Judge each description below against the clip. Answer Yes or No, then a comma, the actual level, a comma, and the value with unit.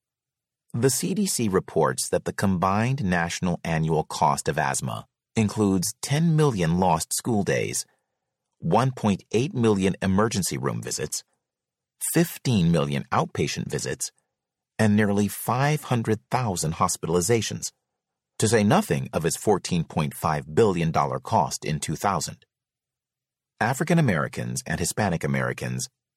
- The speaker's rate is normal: No, slow, 105 wpm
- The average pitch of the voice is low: Yes, low, 105 Hz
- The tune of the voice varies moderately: No, wide, 7.4 semitones